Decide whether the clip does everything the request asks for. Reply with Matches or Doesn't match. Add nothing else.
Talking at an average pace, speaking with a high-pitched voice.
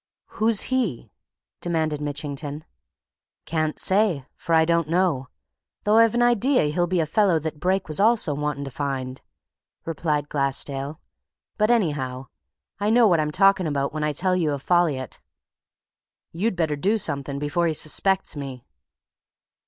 Doesn't match